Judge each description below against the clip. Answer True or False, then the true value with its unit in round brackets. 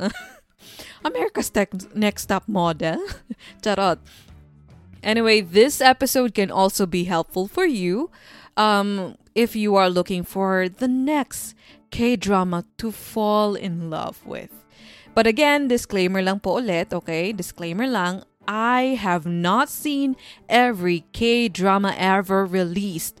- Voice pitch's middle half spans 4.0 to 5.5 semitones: True (4.4 semitones)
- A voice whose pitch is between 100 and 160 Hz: False (195 Hz)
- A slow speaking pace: True (120 wpm)